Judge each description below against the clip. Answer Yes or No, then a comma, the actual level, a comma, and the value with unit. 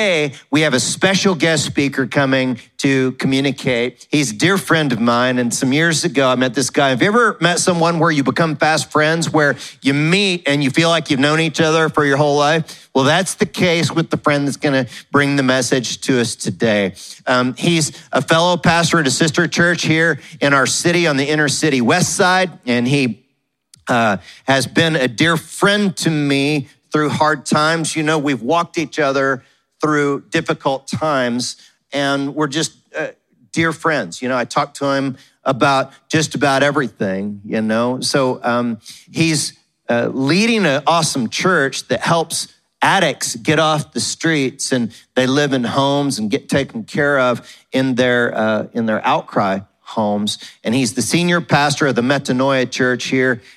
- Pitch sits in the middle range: Yes, medium, 145 Hz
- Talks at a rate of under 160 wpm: No, average, 185 wpm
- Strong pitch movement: No, average, 3.8 semitones